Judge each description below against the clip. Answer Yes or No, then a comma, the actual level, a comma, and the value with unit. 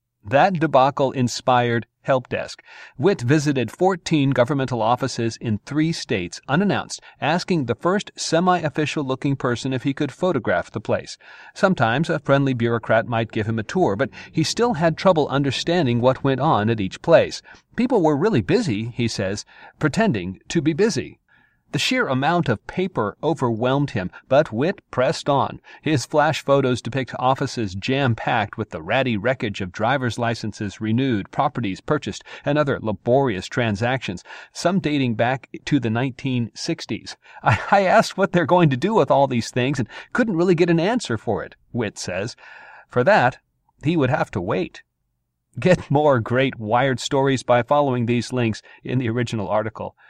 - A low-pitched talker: Yes, low, 130 Hz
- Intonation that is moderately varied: Yes, average, 4.7 semitones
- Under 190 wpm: Yes, average, 165 wpm